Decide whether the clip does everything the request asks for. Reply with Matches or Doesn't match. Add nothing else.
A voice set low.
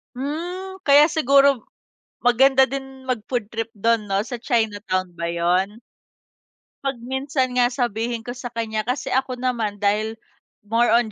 Doesn't match